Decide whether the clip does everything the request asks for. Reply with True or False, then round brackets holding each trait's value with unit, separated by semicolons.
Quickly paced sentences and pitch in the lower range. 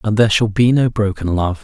True (260 wpm; 105 Hz)